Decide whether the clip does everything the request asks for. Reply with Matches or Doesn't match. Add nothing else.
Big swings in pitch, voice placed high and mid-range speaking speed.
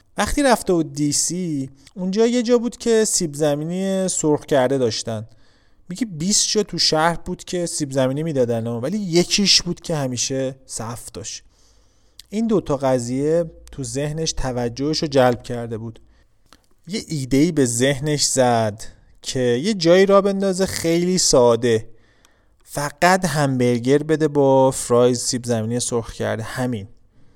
Doesn't match